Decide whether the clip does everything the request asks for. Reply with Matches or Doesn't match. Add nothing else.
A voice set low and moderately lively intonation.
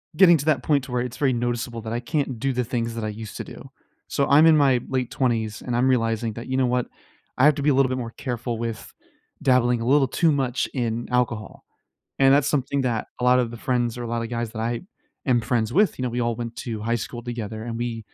Doesn't match